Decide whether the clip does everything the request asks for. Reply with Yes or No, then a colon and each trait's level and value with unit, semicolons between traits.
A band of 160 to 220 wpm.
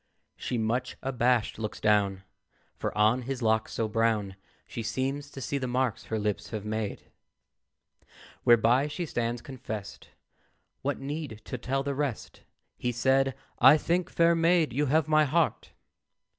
No: average, 150 wpm